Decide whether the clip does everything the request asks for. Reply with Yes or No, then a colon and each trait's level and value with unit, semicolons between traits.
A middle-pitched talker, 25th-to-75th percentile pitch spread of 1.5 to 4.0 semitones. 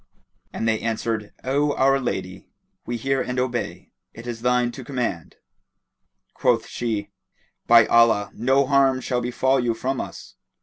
No: low, 120 Hz; narrow, 2.6 semitones